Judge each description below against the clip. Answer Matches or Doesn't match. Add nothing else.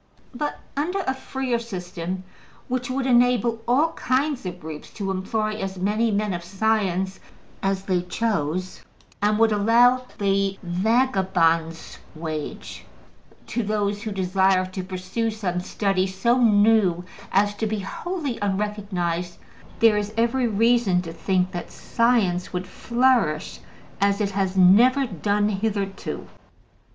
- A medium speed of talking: Doesn't match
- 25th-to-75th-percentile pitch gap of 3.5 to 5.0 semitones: Matches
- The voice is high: Matches